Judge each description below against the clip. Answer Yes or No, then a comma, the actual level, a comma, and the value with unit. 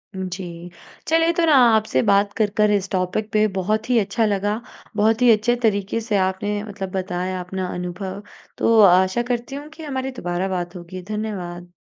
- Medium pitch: No, high, 200 Hz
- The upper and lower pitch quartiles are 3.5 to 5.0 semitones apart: No, average, 3.0 semitones